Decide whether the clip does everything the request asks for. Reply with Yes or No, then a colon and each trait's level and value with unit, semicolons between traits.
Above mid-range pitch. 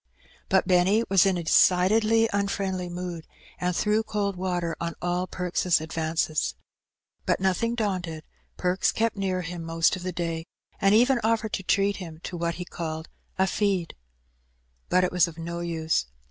No: medium, 180 Hz